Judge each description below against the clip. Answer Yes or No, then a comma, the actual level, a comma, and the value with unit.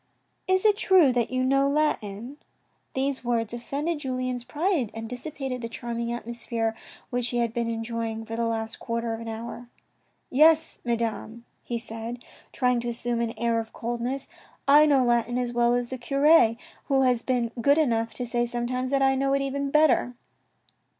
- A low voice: No, high, 240 Hz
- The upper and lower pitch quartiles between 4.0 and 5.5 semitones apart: No, average, 2.8 semitones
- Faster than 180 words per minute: Yes, average, 190 wpm